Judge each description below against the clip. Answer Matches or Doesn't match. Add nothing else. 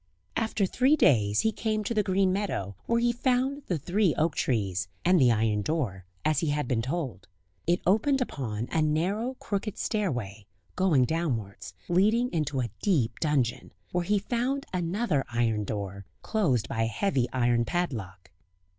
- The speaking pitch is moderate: Matches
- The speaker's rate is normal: Matches